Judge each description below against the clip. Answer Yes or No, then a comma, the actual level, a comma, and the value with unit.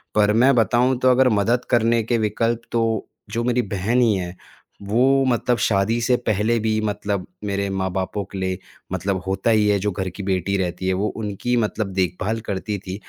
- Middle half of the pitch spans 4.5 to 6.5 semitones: No, average, 3.3 semitones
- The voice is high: No, low, 105 Hz